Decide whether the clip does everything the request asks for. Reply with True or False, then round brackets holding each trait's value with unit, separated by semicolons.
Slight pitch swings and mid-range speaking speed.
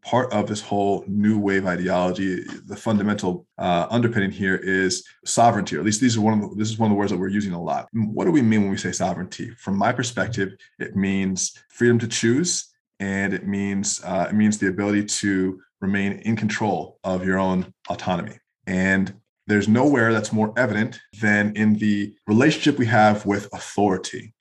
True (2.1 semitones; 195 wpm)